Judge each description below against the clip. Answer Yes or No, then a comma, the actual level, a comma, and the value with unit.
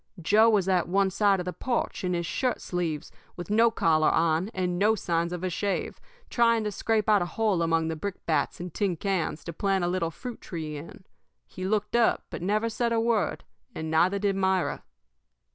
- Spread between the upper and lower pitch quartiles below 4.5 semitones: Yes, average, 3.8 semitones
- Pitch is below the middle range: No, high, 190 Hz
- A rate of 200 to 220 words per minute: Yes, fast, 205 wpm